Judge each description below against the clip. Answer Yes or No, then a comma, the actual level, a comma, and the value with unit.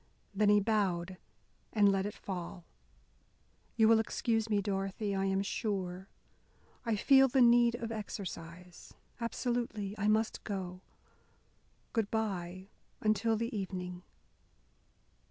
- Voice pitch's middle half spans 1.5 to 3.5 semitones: Yes, average, 2.8 semitones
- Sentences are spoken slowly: Yes, slow, 120 wpm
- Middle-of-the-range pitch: No, high, 205 Hz